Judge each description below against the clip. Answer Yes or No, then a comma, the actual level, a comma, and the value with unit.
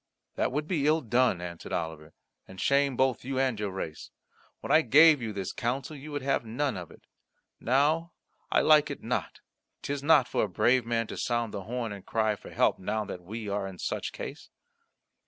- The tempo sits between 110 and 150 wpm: No, fast, 205 wpm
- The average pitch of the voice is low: Yes, low, 120 Hz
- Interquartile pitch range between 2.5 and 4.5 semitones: No, wide, 5.4 semitones